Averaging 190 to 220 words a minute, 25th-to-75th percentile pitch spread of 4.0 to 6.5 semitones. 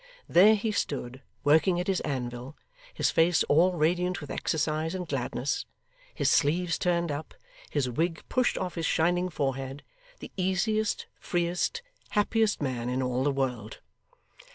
No: average, 145 wpm; average, 4.9 semitones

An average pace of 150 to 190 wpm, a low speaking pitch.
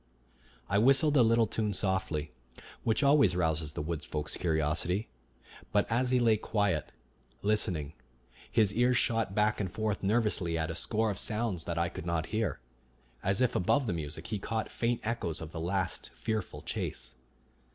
Yes: average, 170 wpm; low, 100 Hz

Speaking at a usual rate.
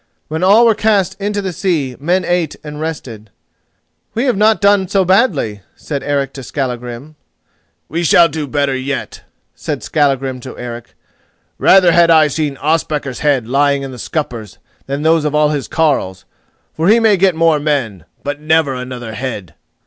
Yes: average, 170 wpm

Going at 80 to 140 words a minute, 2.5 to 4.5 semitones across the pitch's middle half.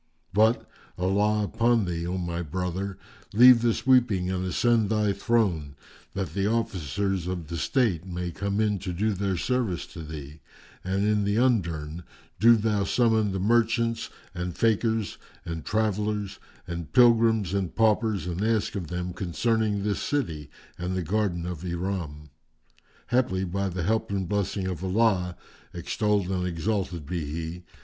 No: average, 155 wpm; average, 3.8 semitones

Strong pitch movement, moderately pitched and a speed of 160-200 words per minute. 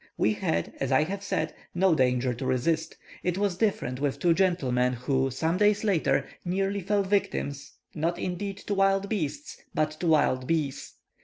Yes: wide, 6.5 semitones; medium, 160 Hz; average, 170 wpm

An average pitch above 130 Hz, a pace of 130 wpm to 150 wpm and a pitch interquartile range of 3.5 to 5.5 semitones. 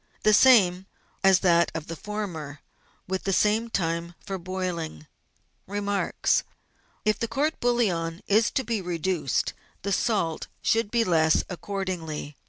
Yes: high, 190 Hz; average, 145 wpm; average, 4.1 semitones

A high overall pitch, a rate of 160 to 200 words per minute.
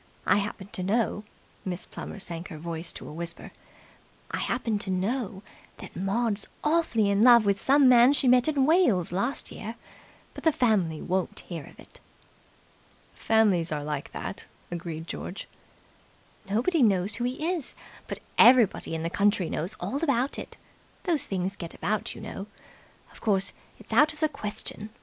Yes: high, 205 Hz; average, 170 wpm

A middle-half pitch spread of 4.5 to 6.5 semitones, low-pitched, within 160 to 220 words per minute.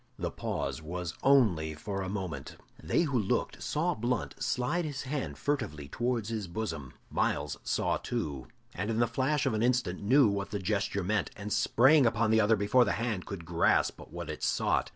Yes: wide, 5.5 semitones; low, 110 Hz; average, 190 wpm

